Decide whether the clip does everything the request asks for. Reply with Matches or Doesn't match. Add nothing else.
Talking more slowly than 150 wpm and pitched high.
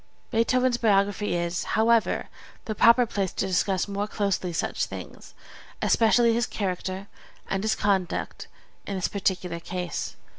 Matches